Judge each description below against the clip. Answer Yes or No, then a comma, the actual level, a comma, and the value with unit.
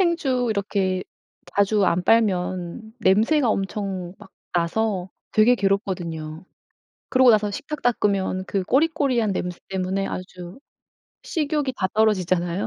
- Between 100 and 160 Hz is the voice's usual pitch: No, high, 200 Hz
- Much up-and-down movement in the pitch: No, average, 3.9 semitones